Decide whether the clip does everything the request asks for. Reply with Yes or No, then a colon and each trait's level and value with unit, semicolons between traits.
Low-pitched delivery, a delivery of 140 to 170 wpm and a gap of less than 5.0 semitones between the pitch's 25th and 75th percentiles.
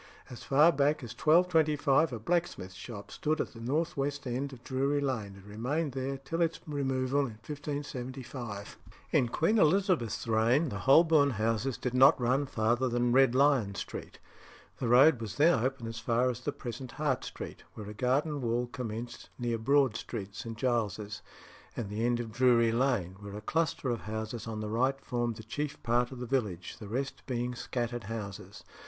No: low, 125 Hz; average, 185 wpm; average, 3.6 semitones